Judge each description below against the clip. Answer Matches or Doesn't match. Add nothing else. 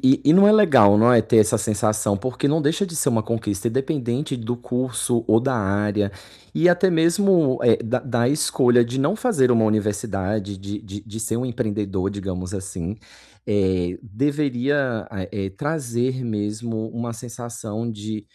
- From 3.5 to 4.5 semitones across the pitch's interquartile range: Matches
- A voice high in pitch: Doesn't match